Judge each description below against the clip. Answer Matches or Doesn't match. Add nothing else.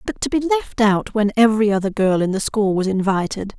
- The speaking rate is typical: Doesn't match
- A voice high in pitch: Matches